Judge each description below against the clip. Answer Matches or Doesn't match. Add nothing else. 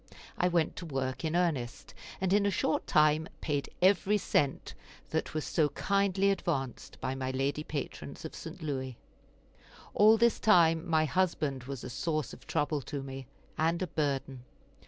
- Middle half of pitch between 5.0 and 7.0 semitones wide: Doesn't match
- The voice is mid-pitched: Matches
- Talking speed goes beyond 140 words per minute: Matches